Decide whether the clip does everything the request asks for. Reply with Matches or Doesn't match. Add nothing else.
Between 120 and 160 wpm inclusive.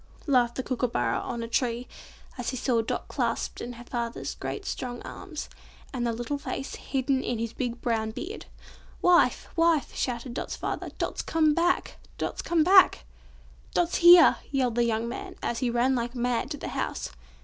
Doesn't match